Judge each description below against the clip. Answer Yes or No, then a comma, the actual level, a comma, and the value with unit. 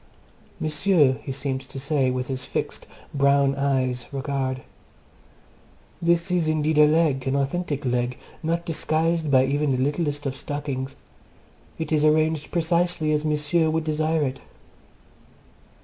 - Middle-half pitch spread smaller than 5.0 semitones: Yes, average, 2.9 semitones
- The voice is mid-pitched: Yes, medium, 145 Hz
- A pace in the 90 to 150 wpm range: Yes, slow, 135 wpm